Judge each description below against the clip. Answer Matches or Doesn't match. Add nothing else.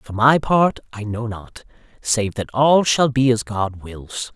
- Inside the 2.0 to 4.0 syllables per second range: Matches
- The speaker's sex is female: Doesn't match